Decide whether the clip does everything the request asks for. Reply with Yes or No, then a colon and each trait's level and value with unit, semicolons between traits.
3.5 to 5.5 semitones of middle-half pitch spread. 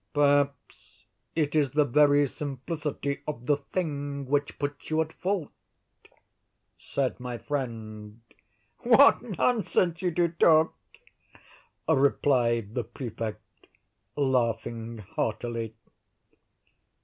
Yes: average, 4.3 semitones